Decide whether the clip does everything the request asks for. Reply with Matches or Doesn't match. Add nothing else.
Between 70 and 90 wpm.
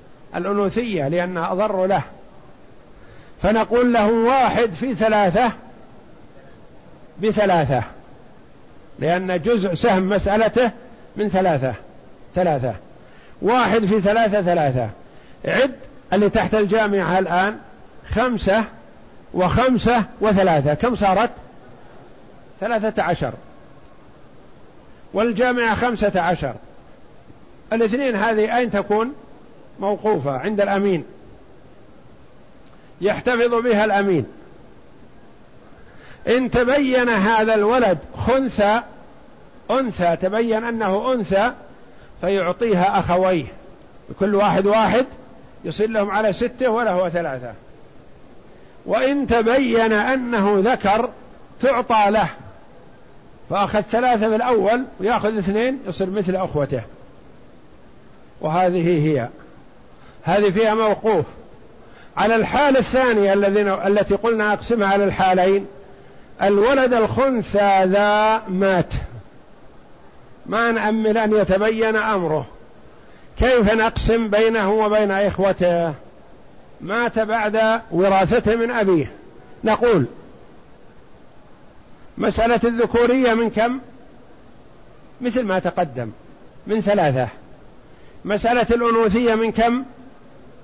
Matches